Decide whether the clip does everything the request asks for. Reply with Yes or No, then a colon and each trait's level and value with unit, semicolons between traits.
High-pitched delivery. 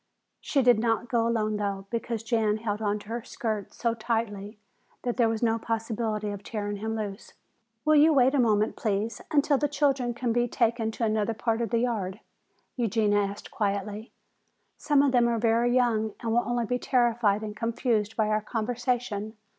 Yes: high, 225 Hz